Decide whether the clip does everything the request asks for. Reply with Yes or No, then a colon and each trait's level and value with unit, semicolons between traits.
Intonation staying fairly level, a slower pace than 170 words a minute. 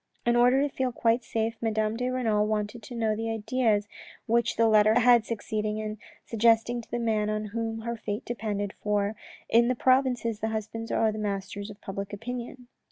No: narrow, 1.9 semitones; average, 190 wpm